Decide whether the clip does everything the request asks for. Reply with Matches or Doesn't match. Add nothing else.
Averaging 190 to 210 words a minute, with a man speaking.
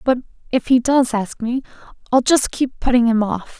Doesn't match